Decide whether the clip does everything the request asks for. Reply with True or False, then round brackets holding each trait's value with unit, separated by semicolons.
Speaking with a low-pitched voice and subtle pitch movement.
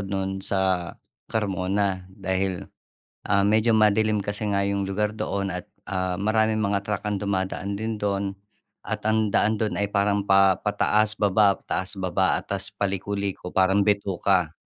True (100 Hz; 1.5 semitones)